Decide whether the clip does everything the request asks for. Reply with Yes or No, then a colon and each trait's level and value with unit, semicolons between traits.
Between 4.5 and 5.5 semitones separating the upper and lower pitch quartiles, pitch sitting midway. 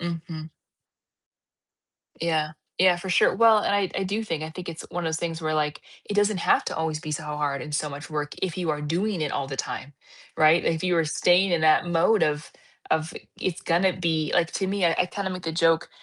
No: average, 2.8 semitones; medium, 165 Hz